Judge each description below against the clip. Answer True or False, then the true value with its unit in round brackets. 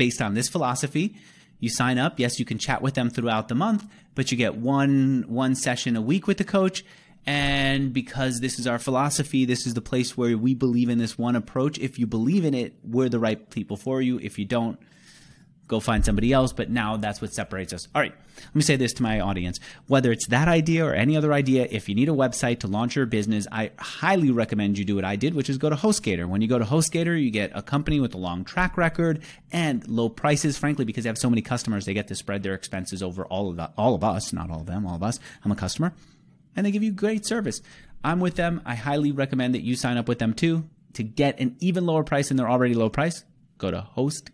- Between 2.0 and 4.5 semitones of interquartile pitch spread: False (4.9 semitones)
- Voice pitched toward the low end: True (125 Hz)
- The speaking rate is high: True (255 wpm)